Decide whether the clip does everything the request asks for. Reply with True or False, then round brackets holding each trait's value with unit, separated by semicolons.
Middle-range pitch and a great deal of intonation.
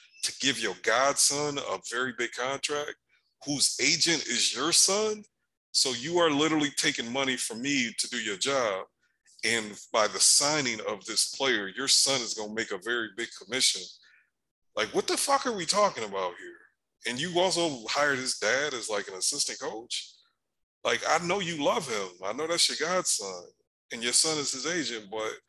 True (145 Hz; 6.6 semitones)